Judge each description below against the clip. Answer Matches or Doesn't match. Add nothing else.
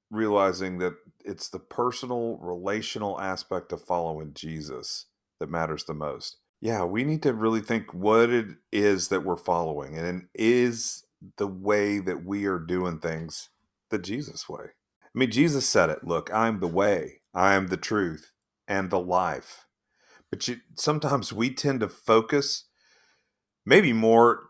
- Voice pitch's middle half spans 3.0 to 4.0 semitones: Doesn't match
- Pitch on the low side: Matches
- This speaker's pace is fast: Doesn't match